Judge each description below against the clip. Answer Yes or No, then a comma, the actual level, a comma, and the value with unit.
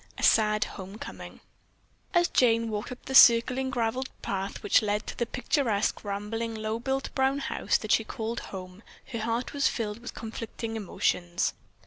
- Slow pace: No, average, 160 wpm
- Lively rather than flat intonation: No, average, 3.1 semitones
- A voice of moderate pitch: No, high, 225 Hz